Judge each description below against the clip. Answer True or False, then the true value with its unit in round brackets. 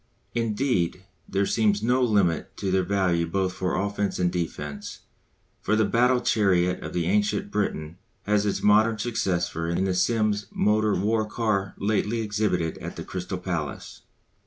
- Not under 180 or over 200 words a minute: False (155 wpm)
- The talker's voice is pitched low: True (100 Hz)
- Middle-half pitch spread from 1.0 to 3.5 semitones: True (3.0 semitones)